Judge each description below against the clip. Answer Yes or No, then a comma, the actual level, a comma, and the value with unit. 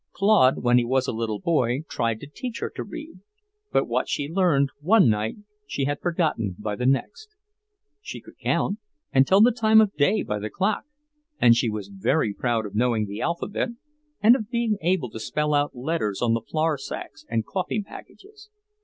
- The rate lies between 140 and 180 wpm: No, average, 195 wpm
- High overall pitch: No, medium, 145 Hz